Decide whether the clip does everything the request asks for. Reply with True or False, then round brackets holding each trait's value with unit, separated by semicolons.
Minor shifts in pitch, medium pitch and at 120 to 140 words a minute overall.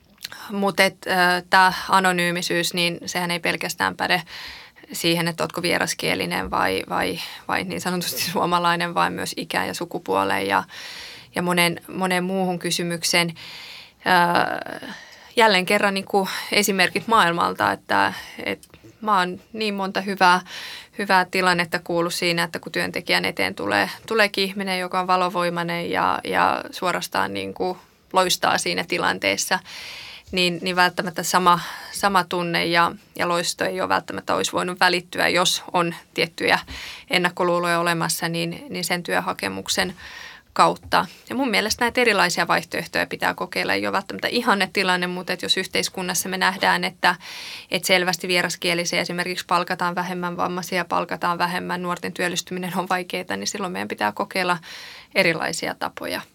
True (1.6 semitones; 180 Hz; 135 wpm)